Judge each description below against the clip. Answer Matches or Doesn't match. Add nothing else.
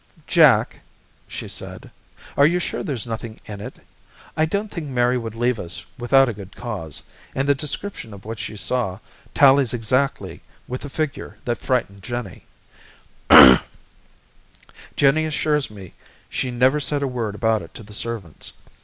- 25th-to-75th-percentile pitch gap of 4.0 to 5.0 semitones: Matches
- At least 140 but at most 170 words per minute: Matches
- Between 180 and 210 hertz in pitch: Doesn't match